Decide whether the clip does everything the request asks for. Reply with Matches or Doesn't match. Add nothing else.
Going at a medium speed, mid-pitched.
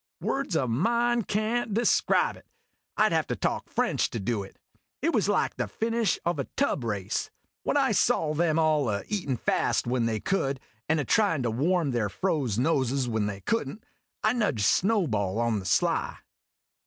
Matches